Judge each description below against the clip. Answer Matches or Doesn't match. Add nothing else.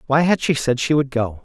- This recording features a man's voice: Matches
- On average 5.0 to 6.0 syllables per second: Matches